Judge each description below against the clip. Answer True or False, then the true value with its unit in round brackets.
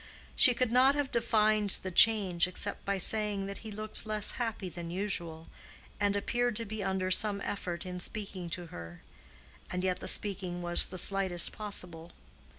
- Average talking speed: True (170 wpm)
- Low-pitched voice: False (200 Hz)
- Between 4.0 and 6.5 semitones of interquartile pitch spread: False (3.1 semitones)